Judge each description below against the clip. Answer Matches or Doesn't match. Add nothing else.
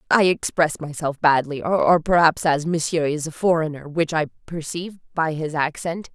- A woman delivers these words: Matches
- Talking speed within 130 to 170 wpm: Matches